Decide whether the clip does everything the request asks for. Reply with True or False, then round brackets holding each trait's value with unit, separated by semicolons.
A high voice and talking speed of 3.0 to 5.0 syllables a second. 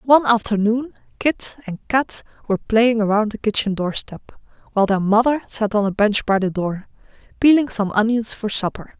False (220 Hz; 5.3 syllables/s)